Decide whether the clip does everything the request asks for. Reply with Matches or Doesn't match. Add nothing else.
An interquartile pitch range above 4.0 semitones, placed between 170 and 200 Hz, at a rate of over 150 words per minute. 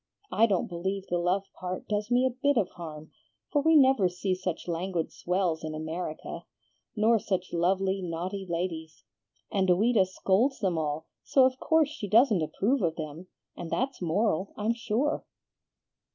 Matches